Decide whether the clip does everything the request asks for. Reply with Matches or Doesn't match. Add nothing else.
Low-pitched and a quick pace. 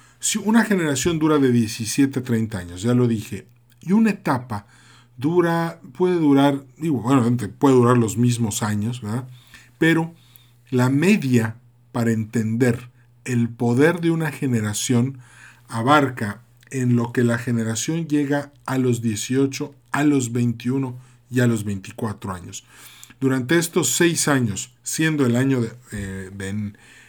Doesn't match